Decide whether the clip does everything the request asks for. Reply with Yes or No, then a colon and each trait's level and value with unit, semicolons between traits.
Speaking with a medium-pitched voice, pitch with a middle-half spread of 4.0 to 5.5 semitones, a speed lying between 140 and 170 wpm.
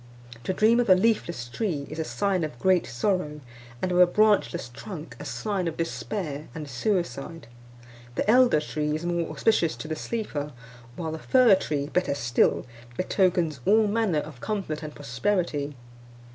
Yes: medium, 170 Hz; average, 5.1 semitones; average, 165 wpm